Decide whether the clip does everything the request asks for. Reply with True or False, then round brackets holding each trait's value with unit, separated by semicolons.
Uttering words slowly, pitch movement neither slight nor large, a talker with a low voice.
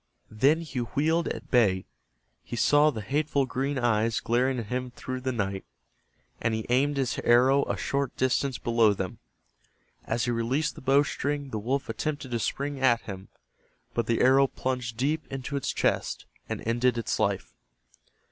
False (170 wpm; 3.2 semitones; 125 Hz)